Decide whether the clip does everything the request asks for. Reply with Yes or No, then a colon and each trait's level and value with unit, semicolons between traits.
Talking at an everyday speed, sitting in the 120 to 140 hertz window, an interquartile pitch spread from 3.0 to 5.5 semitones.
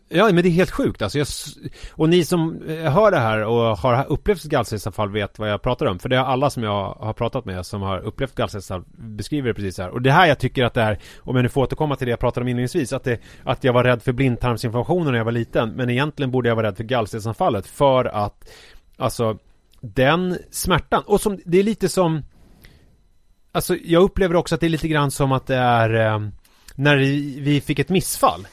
No: fast, 230 wpm; low, 125 Hz; average, 4.9 semitones